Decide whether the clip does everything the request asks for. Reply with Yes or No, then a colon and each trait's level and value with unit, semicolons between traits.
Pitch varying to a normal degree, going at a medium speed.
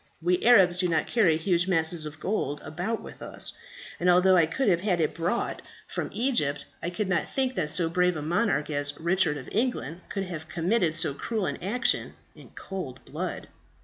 Yes: average, 3.4 semitones; average, 195 wpm